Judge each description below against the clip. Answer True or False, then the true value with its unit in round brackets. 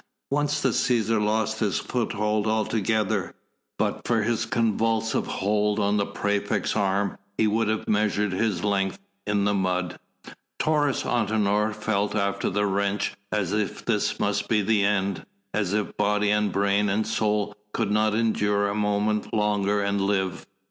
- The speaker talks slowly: False (155 wpm)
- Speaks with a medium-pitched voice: False (105 Hz)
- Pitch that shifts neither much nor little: False (1.4 semitones)